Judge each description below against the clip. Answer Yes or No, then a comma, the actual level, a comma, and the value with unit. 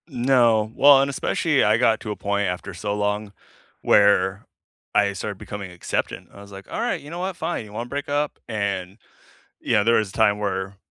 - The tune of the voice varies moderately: Yes, average, 3.8 semitones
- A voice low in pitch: Yes, low, 105 Hz